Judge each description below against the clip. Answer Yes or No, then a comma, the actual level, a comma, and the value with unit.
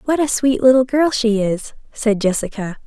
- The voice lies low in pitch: No, high, 235 Hz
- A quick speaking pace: No, average, 190 wpm